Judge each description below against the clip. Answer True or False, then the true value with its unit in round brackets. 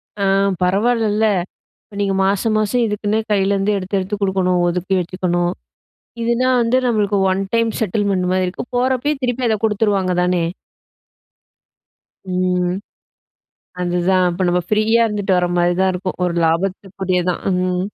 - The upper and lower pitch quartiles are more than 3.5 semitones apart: False (3.0 semitones)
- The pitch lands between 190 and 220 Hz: True (195 Hz)